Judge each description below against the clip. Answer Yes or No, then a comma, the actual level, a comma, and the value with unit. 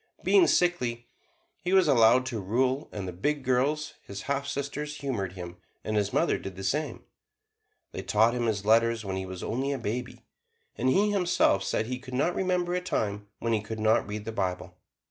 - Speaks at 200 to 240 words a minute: Yes, fast, 205 wpm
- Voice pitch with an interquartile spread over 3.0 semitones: Yes, wide, 5.5 semitones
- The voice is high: No, low, 120 Hz